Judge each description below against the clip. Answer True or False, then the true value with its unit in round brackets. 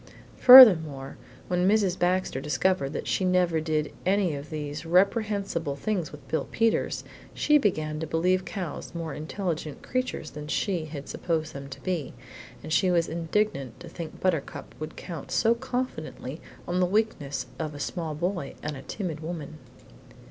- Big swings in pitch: False (3.6 semitones)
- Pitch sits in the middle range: True (165 Hz)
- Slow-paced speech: False (160 wpm)